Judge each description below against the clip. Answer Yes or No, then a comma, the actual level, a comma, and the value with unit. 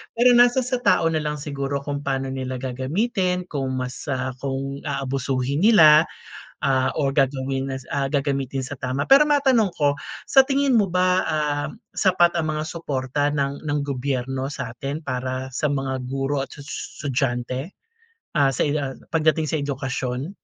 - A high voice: No, medium, 140 Hz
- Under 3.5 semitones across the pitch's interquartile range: Yes, average, 2.9 semitones